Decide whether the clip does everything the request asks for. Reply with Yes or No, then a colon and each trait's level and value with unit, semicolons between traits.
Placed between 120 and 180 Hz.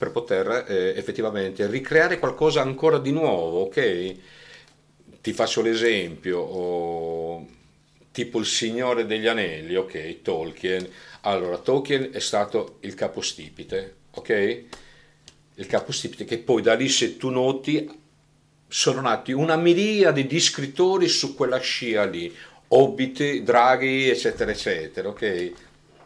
Yes: medium, 140 Hz